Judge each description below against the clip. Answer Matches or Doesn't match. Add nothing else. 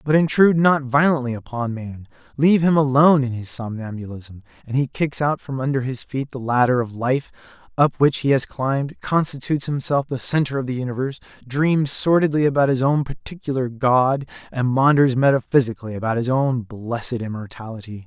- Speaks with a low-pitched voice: Matches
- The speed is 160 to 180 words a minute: Matches